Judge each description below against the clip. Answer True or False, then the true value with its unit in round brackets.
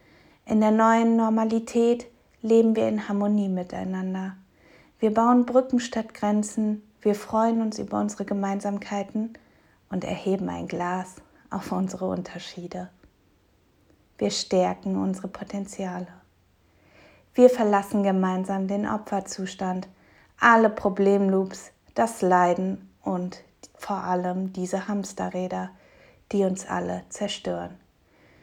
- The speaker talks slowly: True (105 wpm)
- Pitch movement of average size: True (3.0 semitones)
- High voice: True (195 Hz)